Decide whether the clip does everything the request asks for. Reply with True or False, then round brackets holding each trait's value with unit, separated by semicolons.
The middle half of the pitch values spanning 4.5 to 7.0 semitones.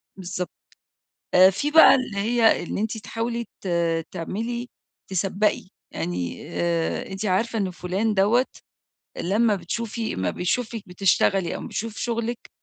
False (4.1 semitones)